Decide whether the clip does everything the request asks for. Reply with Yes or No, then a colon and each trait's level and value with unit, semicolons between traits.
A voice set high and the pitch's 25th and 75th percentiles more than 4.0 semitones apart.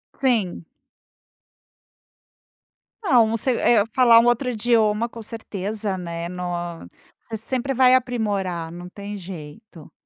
Yes: high, 220 Hz; average, 4.7 semitones